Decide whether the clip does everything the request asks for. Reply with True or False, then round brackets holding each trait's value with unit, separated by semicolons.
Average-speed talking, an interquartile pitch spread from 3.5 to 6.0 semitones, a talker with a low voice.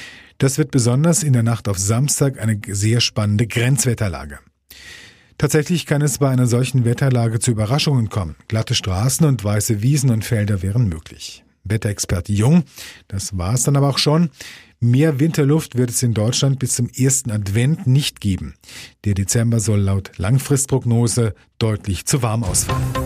True (160 wpm; 4.4 semitones; 120 Hz)